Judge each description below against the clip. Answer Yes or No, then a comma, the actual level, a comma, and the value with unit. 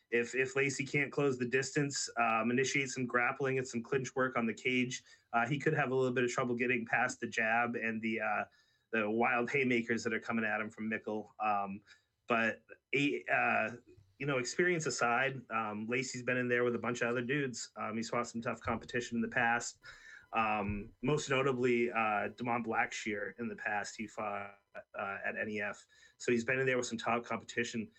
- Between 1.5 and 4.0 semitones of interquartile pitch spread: Yes, narrow, 2.4 semitones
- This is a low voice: Yes, low, 120 Hz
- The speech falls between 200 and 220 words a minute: Yes, fast, 205 wpm